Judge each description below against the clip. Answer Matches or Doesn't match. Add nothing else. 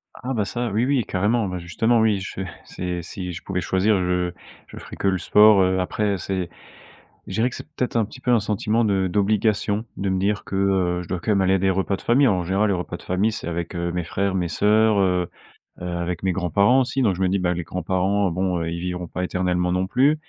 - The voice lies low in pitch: Matches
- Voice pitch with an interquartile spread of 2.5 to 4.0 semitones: Matches